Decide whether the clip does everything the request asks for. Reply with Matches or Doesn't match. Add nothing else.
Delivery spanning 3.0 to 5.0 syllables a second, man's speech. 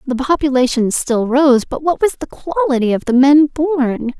Doesn't match